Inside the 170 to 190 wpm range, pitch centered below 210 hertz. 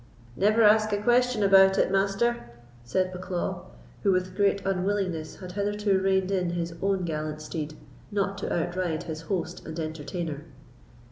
No: average, 150 wpm; medium, 185 Hz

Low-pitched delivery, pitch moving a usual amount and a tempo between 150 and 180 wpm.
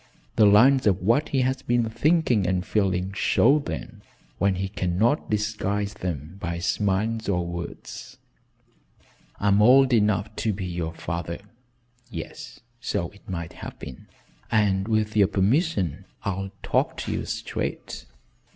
No: low, 100 Hz; average, 3.5 semitones; average, 140 wpm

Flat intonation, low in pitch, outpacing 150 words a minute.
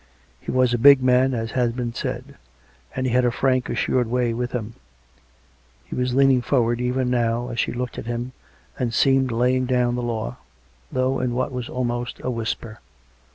Yes: narrow, 1.3 semitones; low, 125 Hz; average, 190 wpm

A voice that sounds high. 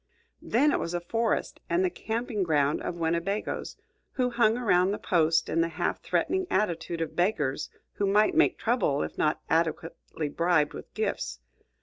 No: medium, 175 Hz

